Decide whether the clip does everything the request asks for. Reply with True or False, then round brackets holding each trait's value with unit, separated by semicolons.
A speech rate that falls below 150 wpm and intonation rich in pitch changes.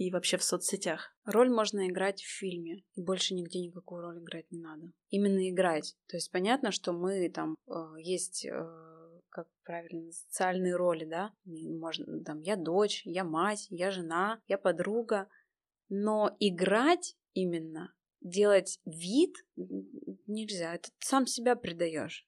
False (140 wpm; 3.2 semitones)